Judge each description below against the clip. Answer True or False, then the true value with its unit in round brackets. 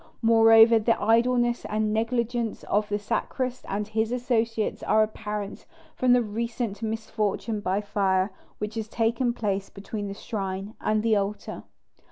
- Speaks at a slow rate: False (145 wpm)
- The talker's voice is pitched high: True (220 Hz)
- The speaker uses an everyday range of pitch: False (1.9 semitones)